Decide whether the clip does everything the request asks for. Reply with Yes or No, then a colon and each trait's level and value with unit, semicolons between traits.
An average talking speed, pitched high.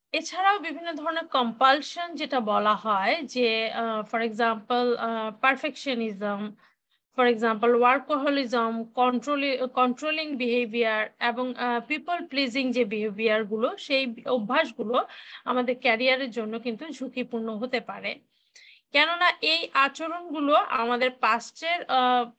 Yes: average, 90 wpm; very high, 250 Hz